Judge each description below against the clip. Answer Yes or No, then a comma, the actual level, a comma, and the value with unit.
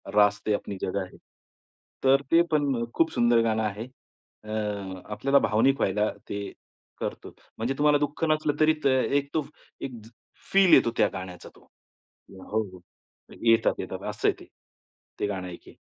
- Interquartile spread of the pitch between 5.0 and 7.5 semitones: Yes, wide, 5.4 semitones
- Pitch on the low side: Yes, low, 115 Hz